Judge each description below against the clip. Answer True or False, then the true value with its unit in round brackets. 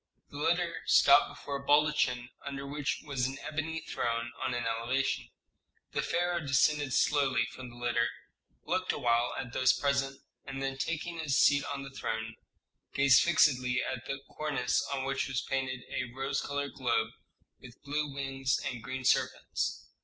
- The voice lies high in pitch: False (135 Hz)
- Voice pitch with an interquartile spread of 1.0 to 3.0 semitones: True (2.5 semitones)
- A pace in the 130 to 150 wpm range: False (160 wpm)